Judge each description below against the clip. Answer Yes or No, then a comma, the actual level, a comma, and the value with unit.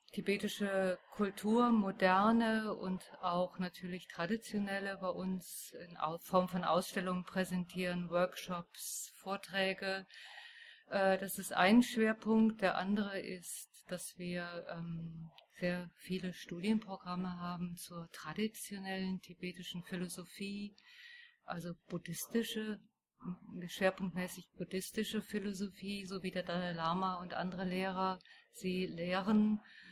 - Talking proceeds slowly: Yes, slow, 95 wpm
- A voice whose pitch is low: No, high, 190 Hz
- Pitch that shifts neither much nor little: No, narrow, 2.3 semitones